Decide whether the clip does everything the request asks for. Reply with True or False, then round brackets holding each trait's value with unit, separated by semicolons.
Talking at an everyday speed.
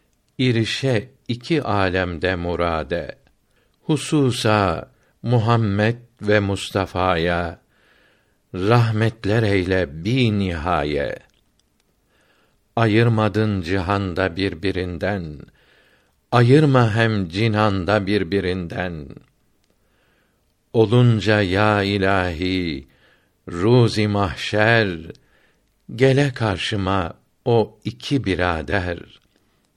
False (60 wpm)